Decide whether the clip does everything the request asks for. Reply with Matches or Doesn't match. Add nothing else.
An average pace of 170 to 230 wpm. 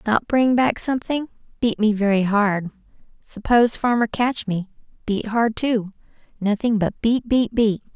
Doesn't match